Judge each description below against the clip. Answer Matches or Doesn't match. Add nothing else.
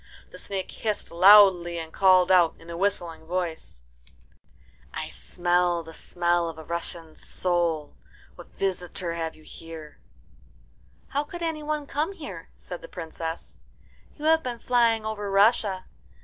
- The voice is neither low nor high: Matches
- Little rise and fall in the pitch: Doesn't match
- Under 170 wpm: Matches